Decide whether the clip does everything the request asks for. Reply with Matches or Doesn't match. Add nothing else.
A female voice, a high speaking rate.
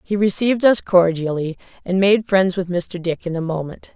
Doesn't match